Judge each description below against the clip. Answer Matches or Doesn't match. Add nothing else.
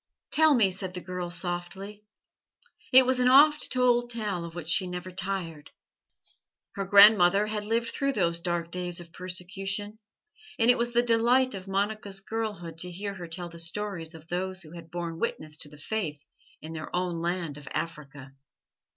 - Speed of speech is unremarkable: Matches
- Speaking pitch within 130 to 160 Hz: Doesn't match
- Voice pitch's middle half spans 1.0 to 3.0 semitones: Doesn't match